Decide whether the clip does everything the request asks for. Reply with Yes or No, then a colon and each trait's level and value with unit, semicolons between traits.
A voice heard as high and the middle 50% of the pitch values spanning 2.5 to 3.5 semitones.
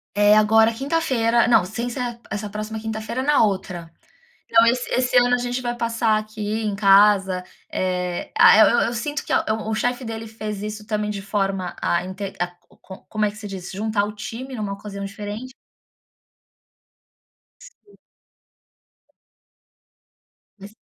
Yes: high, 215 Hz; average, 2.8 semitones